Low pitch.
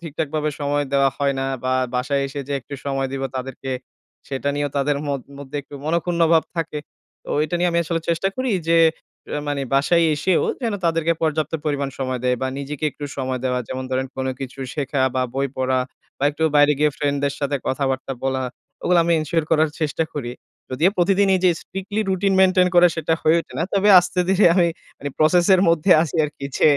No: medium, 150 Hz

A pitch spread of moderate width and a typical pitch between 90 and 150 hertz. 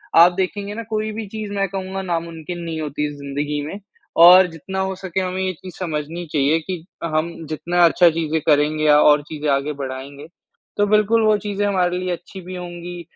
No: average, 3.7 semitones; medium, 175 Hz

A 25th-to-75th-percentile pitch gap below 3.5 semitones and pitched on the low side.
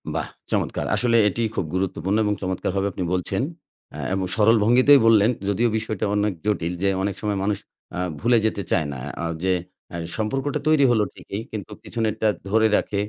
Yes: average, 2.9 semitones; low, 105 Hz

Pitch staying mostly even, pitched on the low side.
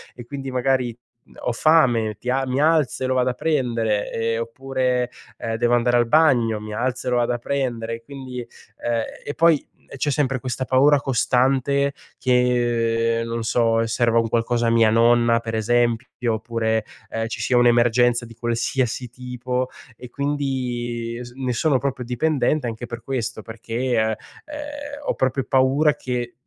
Yes: narrow, 2.3 semitones; low, 120 Hz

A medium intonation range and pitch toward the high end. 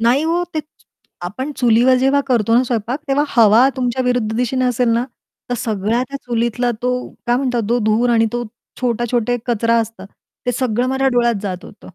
No: narrow, 1.9 semitones; high, 240 Hz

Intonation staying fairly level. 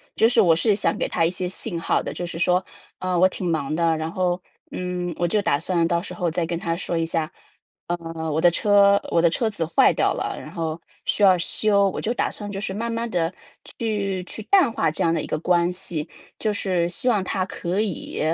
No: average, 3.2 semitones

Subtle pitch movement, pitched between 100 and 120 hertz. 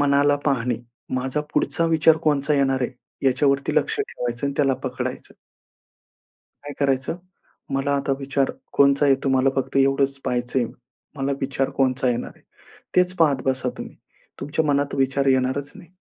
No: narrow, 1.3 semitones; low, 135 Hz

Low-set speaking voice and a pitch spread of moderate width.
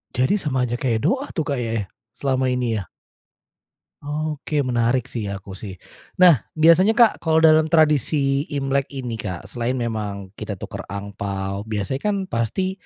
No: low, 130 Hz; wide, 6.2 semitones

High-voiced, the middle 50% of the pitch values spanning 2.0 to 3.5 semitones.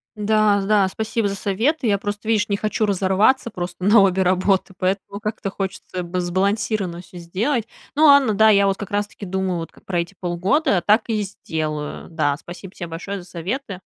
Yes: high, 195 Hz; average, 2.8 semitones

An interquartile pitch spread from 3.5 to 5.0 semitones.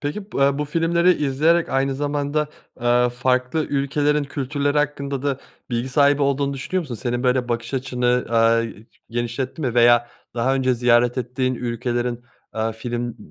No: average, 3.0 semitones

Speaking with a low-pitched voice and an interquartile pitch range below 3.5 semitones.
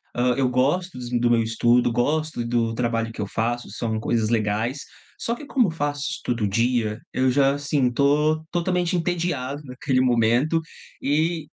No: low, 125 Hz; average, 4.4 semitones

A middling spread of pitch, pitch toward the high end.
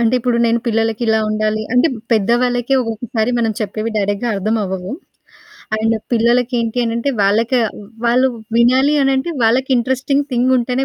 No: narrow, 2.2 semitones; high, 235 Hz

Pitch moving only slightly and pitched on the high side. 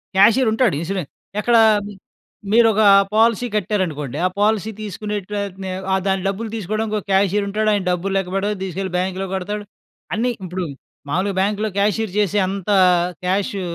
Yes: narrow, 2.2 semitones; high, 200 Hz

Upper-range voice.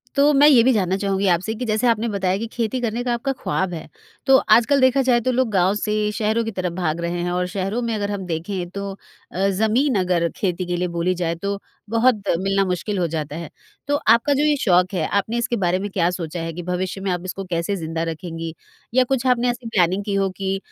Yes: high, 195 Hz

